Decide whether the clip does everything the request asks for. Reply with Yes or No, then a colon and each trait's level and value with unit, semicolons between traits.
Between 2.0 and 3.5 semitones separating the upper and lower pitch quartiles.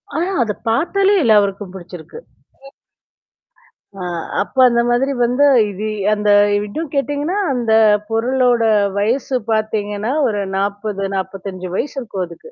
No: average, 4.2 semitones